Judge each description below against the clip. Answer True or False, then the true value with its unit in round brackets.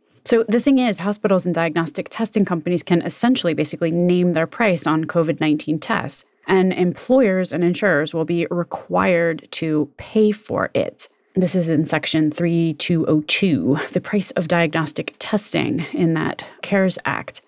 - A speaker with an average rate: True (150 wpm)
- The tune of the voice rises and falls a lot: False (3.7 semitones)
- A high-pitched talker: False (175 Hz)